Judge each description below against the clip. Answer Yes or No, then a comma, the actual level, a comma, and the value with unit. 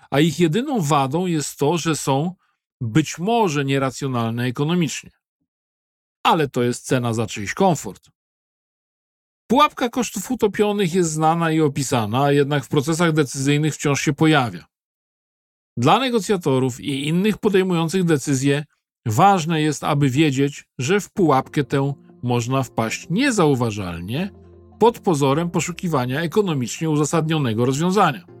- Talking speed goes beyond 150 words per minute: No, average, 120 wpm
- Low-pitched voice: No, medium, 155 Hz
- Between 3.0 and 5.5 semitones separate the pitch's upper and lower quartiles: Yes, average, 4.7 semitones